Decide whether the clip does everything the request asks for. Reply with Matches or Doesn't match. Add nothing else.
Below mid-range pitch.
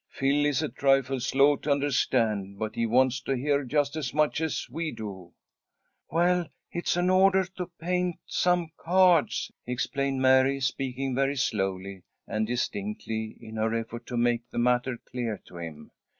Matches